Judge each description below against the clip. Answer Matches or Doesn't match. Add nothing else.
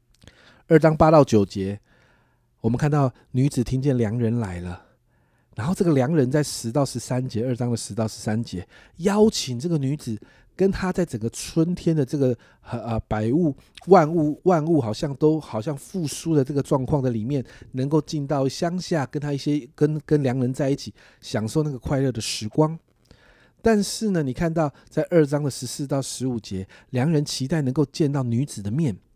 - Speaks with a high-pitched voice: Doesn't match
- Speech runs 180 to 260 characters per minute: Doesn't match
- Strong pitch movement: Doesn't match